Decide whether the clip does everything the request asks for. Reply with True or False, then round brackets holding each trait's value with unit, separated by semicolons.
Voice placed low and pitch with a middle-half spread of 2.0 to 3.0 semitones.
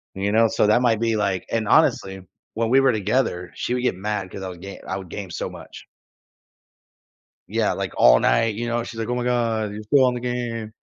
False (110 Hz; 3.4 semitones)